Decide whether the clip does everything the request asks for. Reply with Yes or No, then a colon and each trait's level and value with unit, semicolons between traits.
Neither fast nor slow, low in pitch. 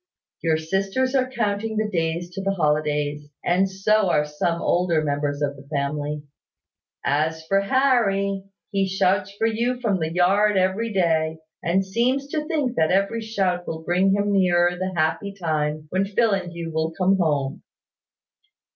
No: average, 160 wpm; medium, 185 Hz